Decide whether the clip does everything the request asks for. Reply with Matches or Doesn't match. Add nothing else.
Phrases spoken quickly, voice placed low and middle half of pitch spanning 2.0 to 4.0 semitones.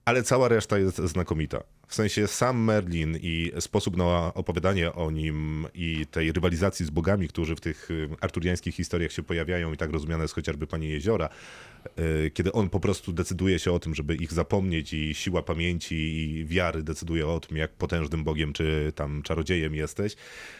Matches